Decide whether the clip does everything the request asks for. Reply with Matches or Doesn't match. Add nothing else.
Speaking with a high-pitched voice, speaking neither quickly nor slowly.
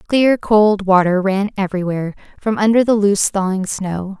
Matches